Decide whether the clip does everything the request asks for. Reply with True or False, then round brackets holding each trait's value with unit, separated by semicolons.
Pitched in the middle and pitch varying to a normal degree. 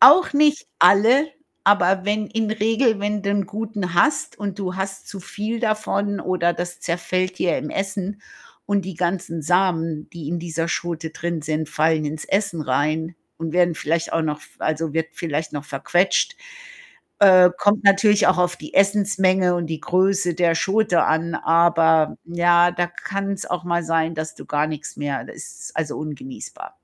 True (175 Hz; 3.6 semitones)